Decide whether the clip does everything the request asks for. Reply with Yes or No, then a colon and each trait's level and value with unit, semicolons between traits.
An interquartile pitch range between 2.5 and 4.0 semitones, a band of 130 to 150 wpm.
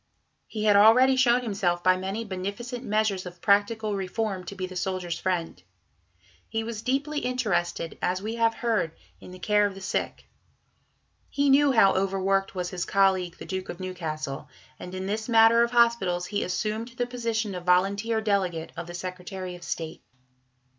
No: average, 3.7 semitones; average, 180 wpm